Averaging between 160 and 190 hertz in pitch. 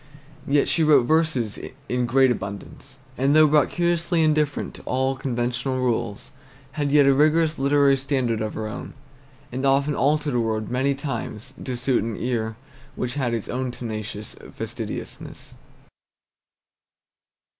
No: low, 130 Hz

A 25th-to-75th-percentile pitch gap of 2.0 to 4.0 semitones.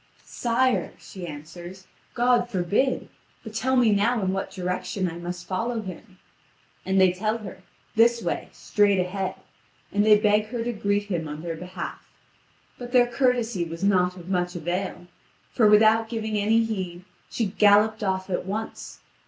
Yes: average, 3.6 semitones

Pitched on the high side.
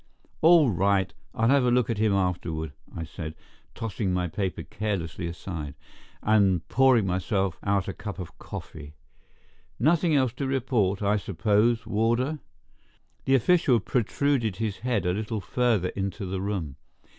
No: low, 105 Hz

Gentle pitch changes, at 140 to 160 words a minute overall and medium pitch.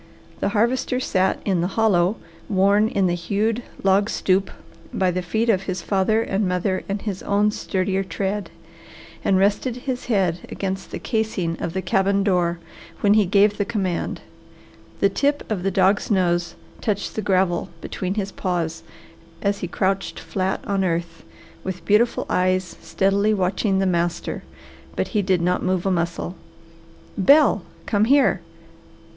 No: narrow, 2.2 semitones; average, 155 wpm; high, 195 Hz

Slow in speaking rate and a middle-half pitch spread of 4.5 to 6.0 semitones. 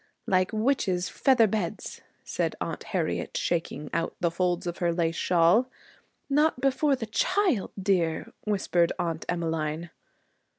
Yes: slow, 130 wpm; average, 5.3 semitones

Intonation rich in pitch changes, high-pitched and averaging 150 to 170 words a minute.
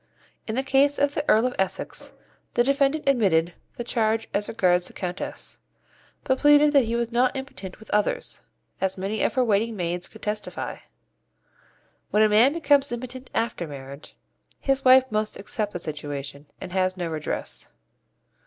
Yes: wide, 6.2 semitones; high, 220 Hz; average, 165 wpm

